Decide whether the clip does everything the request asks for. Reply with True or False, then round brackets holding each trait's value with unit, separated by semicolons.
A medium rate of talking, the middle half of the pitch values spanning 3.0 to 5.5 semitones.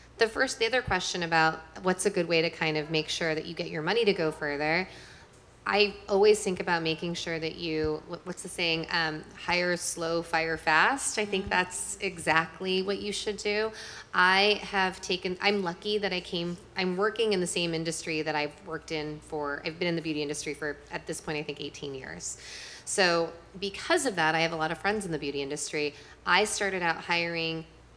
False (210 wpm; 3.4 semitones)